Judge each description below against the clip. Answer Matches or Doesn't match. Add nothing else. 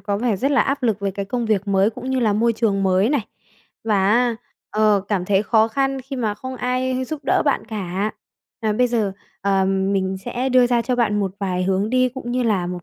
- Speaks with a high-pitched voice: Matches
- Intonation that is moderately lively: Matches